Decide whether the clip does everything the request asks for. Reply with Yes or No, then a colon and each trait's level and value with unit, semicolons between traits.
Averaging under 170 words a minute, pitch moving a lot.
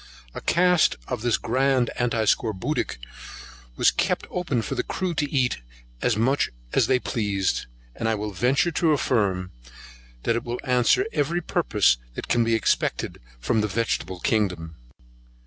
No: average, 155 wpm; average, 4.4 semitones